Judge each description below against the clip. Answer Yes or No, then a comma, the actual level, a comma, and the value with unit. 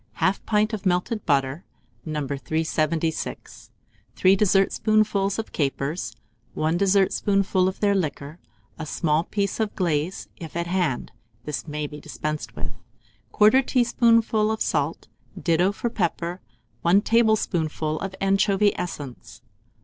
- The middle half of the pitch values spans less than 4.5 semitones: No, average, 4.9 semitones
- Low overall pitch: No, medium, 185 Hz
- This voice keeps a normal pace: No, slow, 125 wpm